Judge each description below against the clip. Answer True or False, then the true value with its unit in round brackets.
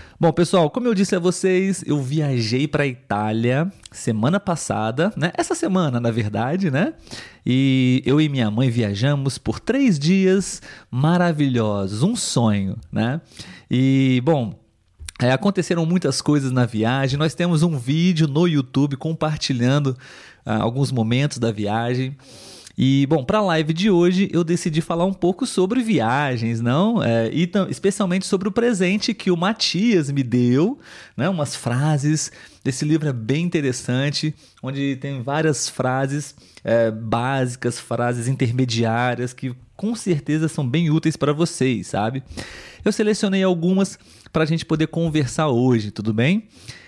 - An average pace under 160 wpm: True (145 wpm)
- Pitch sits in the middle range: True (145 Hz)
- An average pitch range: False (6.1 semitones)